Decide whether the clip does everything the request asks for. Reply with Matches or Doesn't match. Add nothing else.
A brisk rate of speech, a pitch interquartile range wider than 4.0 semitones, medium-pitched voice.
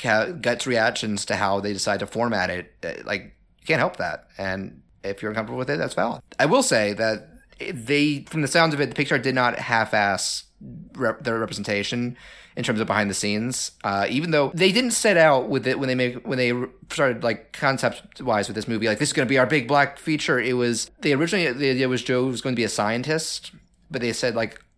Doesn't match